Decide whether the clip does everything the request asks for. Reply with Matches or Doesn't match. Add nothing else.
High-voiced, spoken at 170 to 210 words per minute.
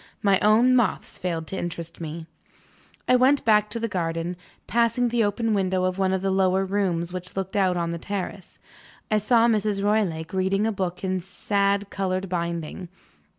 Matches